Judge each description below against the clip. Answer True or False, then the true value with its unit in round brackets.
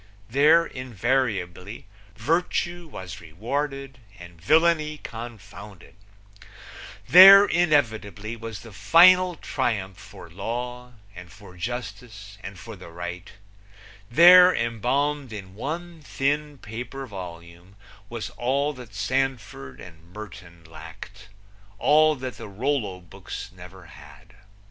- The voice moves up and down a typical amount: False (7.1 semitones)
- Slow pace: True (105 wpm)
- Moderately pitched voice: False (115 Hz)